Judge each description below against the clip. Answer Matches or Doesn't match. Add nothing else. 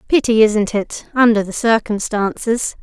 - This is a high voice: Matches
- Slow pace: Matches